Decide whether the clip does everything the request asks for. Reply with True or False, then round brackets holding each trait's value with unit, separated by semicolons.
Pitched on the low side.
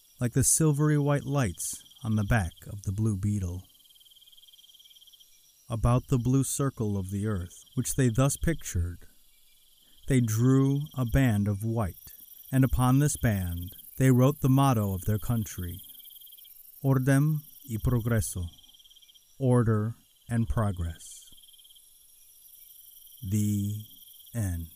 True (110 Hz)